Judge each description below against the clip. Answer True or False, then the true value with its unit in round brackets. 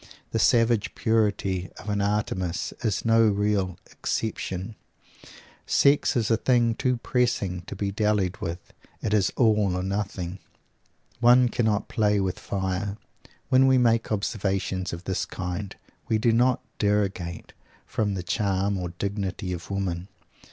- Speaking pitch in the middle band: False (100 Hz)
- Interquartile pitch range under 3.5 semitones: True (3.1 semitones)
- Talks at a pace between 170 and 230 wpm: False (140 wpm)